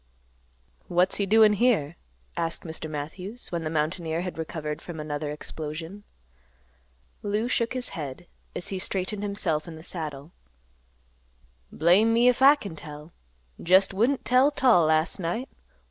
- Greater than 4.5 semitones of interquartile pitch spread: Yes, average, 5.0 semitones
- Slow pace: No, average, 145 wpm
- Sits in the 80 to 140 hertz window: No, medium, 175 Hz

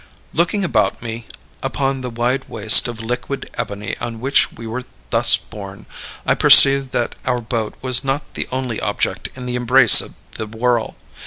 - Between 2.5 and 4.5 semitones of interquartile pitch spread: Yes, average, 2.8 semitones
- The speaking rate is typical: Yes, average, 170 wpm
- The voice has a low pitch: Yes, low, 120 Hz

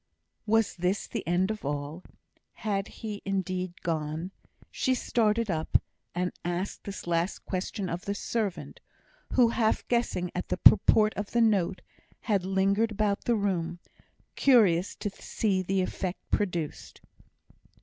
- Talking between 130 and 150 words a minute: Yes, average, 140 wpm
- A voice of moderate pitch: No, high, 195 Hz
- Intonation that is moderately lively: Yes, average, 3.3 semitones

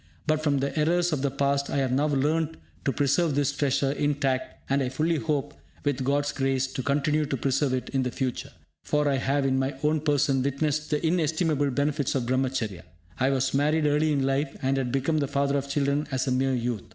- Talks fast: Yes, fast, 220 wpm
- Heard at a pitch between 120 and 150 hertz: Yes, medium, 140 Hz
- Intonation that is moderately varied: No, narrow, 1.9 semitones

